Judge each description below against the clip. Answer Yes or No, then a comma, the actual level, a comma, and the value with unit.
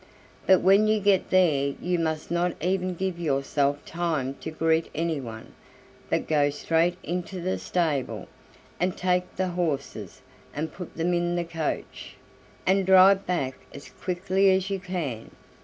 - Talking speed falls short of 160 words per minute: Yes, average, 150 wpm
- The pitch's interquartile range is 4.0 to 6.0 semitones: No, average, 3.3 semitones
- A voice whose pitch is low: No, medium, 175 Hz